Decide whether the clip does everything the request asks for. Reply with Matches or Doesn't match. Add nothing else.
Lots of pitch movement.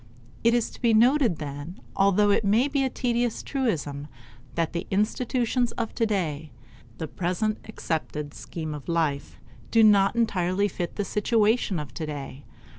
Matches